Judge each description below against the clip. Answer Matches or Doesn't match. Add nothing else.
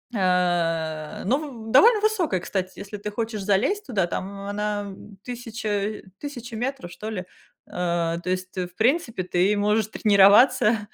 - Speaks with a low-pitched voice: Doesn't match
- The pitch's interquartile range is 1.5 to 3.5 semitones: Doesn't match